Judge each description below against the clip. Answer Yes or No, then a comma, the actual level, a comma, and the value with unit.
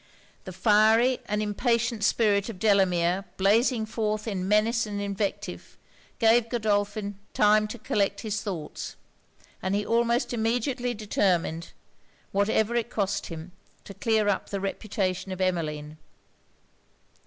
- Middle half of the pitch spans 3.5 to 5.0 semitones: No, narrow, 2.6 semitones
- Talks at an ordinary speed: No, slow, 125 wpm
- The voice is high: Yes, high, 210 Hz